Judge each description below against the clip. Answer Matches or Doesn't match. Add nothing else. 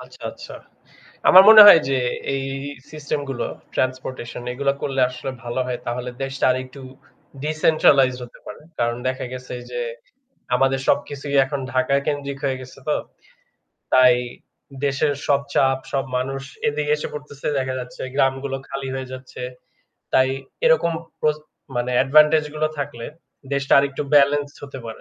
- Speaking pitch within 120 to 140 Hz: Matches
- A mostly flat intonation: Matches